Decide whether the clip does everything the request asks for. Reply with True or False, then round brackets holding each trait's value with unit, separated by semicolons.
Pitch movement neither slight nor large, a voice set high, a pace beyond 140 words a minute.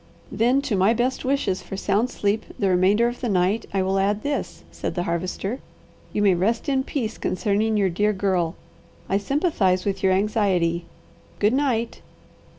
True (3.8 semitones; 205 Hz; 170 wpm)